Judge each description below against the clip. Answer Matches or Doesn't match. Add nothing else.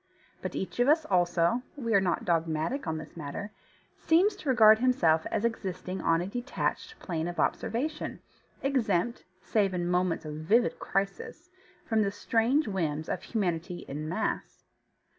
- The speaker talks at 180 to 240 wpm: Doesn't match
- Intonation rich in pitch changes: Matches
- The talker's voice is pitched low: Doesn't match